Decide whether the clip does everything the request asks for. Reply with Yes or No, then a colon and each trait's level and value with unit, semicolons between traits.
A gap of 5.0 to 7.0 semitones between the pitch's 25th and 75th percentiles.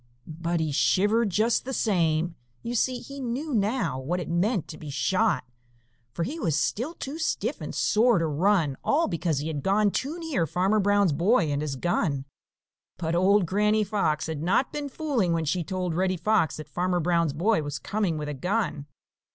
Yes: average, 5.3 semitones